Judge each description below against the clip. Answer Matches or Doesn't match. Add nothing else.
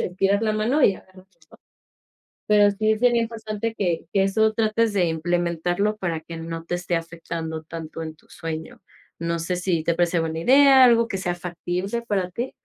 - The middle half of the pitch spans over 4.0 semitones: Matches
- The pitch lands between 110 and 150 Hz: Doesn't match